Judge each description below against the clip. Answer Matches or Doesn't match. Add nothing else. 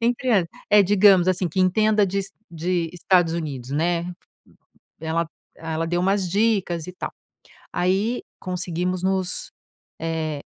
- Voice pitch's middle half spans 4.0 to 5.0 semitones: Doesn't match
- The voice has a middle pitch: Matches